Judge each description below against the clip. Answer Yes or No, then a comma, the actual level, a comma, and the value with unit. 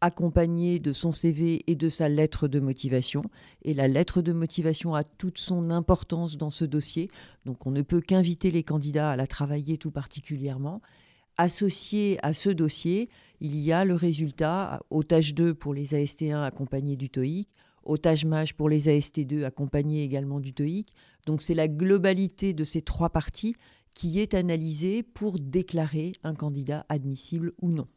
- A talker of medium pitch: Yes, medium, 160 Hz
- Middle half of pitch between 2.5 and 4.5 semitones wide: Yes, average, 2.8 semitones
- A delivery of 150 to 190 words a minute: Yes, average, 165 wpm